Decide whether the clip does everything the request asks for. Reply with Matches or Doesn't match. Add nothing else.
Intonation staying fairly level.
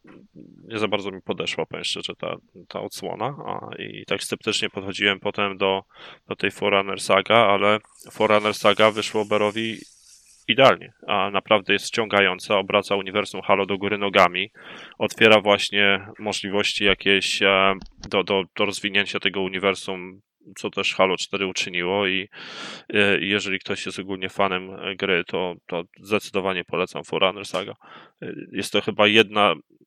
Matches